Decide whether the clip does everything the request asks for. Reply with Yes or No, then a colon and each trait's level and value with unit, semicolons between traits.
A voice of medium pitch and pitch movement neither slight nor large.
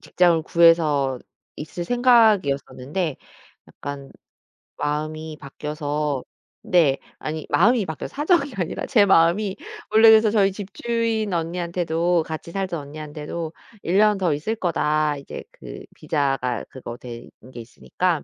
Yes: medium, 165 Hz; average, 4.9 semitones